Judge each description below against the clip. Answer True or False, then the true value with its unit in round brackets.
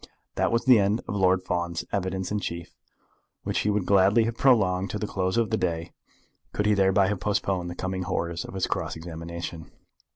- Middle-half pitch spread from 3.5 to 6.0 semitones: False (2.9 semitones)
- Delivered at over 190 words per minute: True (200 wpm)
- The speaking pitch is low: True (95 Hz)